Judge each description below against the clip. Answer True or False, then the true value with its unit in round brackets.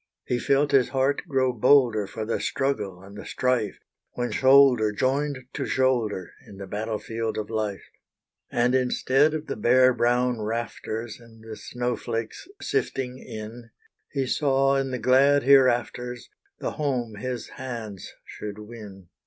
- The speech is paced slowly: False (145 wpm)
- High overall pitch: False (120 Hz)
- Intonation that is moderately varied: True (3.2 semitones)